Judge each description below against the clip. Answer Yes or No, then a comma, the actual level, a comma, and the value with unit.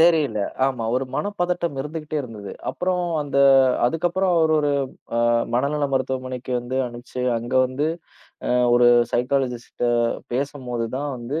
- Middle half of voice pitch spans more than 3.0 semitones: Yes, average, 4.1 semitones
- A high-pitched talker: No, low, 135 Hz